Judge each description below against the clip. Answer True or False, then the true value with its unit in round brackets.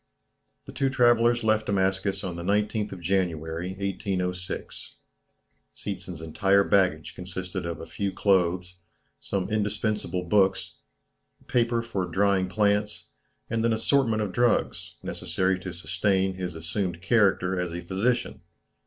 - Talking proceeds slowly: True (125 wpm)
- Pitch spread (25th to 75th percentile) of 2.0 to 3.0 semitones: True (2.7 semitones)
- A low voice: True (95 Hz)